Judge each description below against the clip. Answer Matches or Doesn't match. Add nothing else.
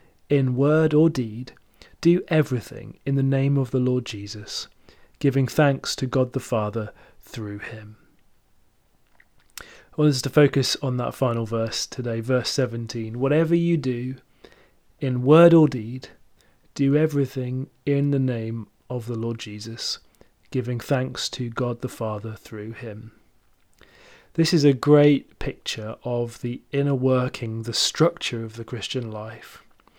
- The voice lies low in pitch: Matches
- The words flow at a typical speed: Matches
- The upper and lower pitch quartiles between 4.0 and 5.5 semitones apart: Doesn't match